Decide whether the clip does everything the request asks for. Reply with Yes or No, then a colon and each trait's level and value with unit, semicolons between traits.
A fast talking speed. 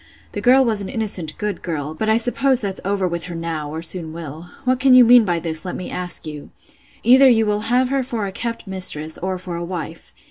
Yes: fast, 240 wpm